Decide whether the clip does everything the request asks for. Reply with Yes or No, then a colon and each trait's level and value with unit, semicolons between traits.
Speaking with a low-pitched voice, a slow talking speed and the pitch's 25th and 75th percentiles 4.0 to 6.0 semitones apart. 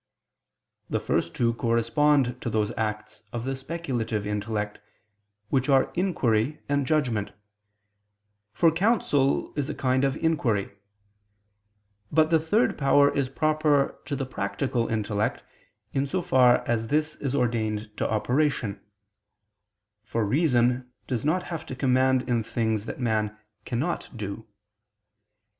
Yes: low, 125 Hz; slow, 125 wpm; average, 4.7 semitones